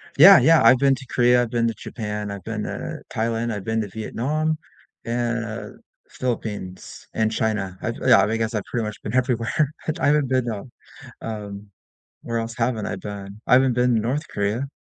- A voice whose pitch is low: Yes, low, 115 Hz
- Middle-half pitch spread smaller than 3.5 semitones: Yes, average, 2.9 semitones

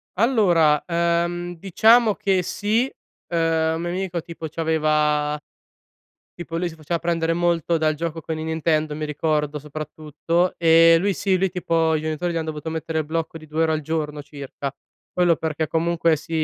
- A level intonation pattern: Yes, narrow, 1.9 semitones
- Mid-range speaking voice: Yes, medium, 165 Hz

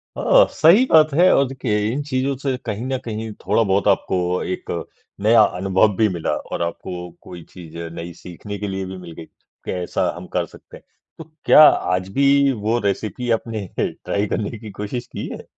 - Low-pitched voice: Yes, low, 105 Hz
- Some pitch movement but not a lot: No, wide, 5.9 semitones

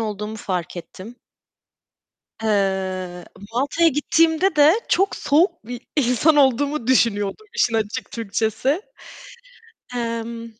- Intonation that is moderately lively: No, wide, 5.8 semitones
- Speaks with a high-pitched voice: Yes, high, 235 Hz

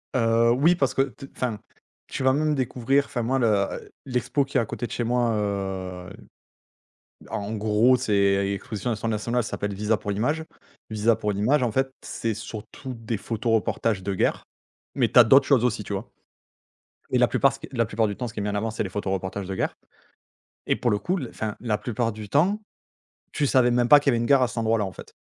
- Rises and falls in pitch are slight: No, average, 3.5 semitones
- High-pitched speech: No, low, 115 Hz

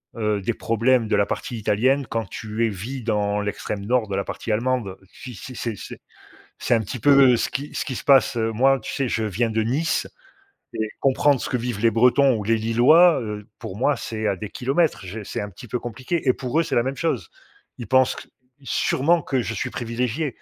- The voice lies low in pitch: Yes, low, 120 Hz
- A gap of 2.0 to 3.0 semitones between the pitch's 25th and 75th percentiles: No, average, 3.4 semitones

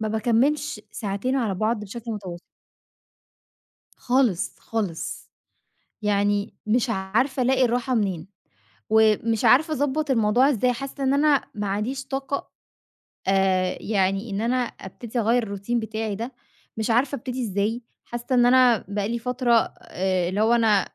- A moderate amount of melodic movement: Yes, average, 3.6 semitones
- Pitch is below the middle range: No, high, 225 Hz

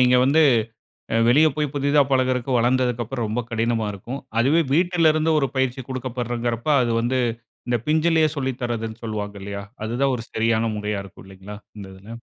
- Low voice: Yes, low, 120 Hz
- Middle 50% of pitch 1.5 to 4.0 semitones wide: Yes, average, 3.4 semitones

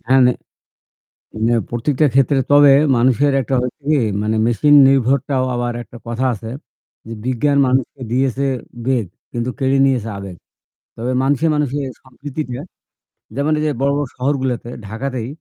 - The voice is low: Yes, low, 130 Hz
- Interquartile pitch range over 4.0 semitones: No, average, 2.7 semitones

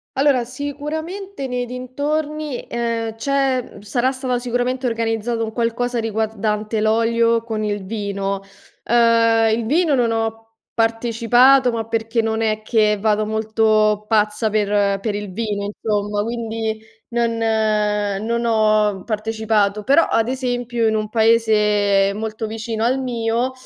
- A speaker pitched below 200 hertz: No, high, 225 Hz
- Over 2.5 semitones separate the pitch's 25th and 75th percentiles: No, narrow, 2.2 semitones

